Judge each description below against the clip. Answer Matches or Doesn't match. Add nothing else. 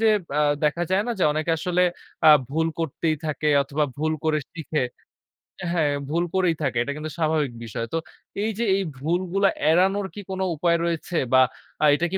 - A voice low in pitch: Doesn't match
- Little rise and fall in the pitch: Doesn't match